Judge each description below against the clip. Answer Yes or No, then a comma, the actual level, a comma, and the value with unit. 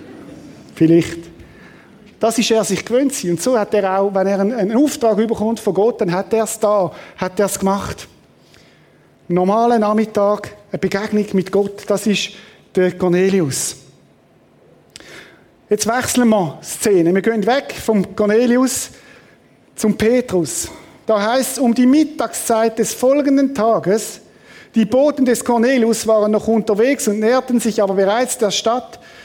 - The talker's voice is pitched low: No, high, 215 Hz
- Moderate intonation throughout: Yes, average, 3.1 semitones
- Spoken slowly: No, average, 150 wpm